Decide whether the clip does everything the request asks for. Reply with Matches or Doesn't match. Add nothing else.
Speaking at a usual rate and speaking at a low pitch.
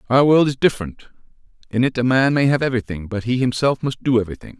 Doesn't match